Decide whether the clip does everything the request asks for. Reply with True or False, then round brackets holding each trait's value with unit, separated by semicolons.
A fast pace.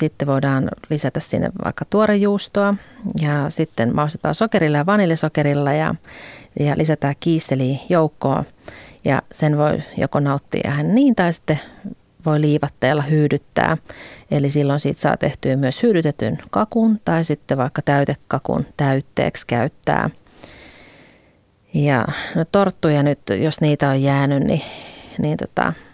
False (125 wpm)